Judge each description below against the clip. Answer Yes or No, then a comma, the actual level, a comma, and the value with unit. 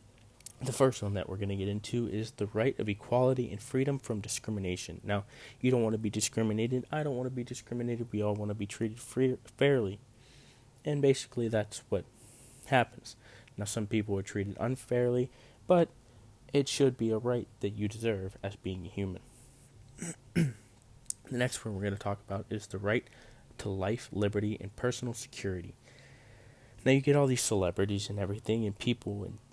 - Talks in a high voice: No, low, 115 Hz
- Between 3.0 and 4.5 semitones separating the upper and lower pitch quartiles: Yes, average, 3.5 semitones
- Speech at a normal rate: Yes, average, 185 wpm